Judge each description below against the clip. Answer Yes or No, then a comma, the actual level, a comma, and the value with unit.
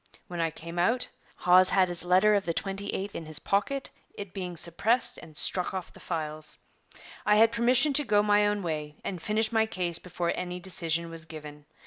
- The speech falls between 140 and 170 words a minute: No, average, 195 wpm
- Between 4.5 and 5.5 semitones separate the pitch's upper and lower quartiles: No, average, 3.9 semitones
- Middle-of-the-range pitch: Yes, medium, 180 Hz